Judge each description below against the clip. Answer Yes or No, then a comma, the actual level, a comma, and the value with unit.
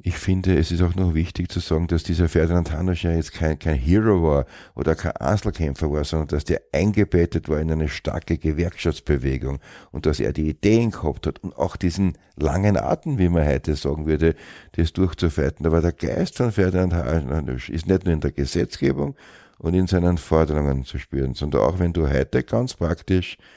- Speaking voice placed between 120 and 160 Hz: No, very low, 85 Hz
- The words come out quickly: Yes, fast, 195 wpm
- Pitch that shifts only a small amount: No, average, 3.0 semitones